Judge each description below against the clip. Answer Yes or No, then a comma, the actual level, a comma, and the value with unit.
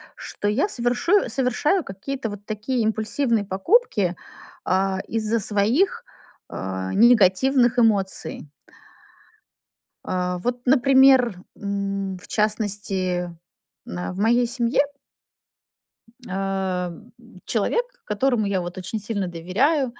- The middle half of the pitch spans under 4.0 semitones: No, average, 4.4 semitones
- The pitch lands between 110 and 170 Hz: No, high, 210 Hz